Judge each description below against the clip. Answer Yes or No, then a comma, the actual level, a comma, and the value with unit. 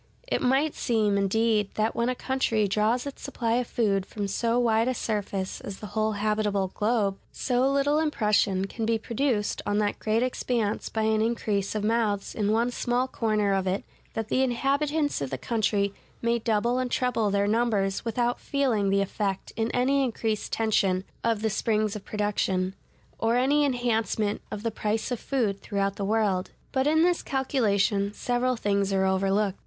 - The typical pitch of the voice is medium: No, high, 220 Hz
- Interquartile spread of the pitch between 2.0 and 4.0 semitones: Yes, average, 3.3 semitones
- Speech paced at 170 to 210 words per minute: Yes, average, 180 wpm